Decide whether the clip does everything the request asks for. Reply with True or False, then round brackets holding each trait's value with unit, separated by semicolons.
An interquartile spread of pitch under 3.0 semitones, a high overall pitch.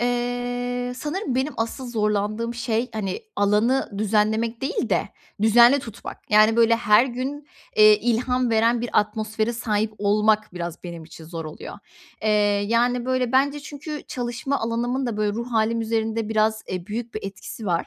True (2.5 semitones; 230 Hz)